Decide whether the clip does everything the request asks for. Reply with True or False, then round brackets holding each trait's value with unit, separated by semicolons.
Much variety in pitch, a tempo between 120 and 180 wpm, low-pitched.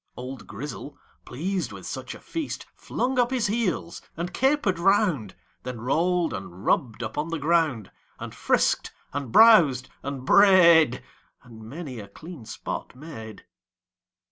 False (6.8 semitones; 140 wpm; 150 Hz)